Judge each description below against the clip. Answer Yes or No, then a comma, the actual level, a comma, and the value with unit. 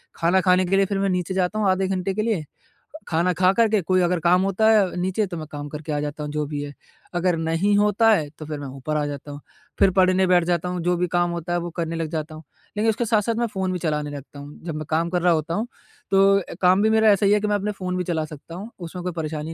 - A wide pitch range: No, average, 3.6 semitones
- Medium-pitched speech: Yes, medium, 180 Hz